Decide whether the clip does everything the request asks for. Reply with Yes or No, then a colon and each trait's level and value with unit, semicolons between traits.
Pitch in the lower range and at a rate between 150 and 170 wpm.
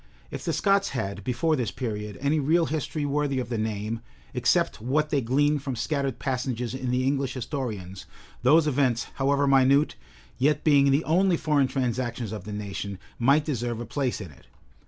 No: low, 130 Hz; average, 180 wpm